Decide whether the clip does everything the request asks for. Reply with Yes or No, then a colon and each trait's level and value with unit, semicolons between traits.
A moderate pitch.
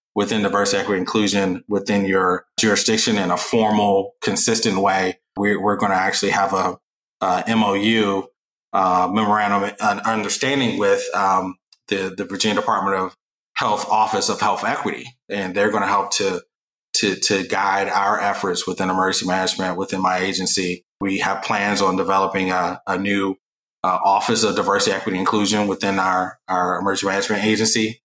No: low, 100 Hz